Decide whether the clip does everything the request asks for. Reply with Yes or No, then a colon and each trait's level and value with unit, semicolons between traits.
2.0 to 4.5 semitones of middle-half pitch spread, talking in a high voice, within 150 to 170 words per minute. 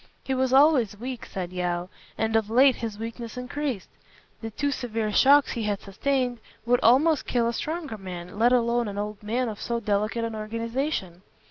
No: average, 3.4 semitones; high, 230 Hz; average, 185 wpm